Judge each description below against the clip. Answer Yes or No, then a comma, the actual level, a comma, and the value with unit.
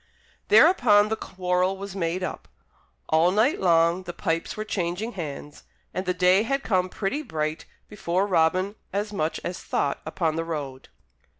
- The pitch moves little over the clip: No, average, 3.7 semitones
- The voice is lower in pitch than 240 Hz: Yes, medium, 185 Hz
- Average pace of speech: Yes, average, 160 wpm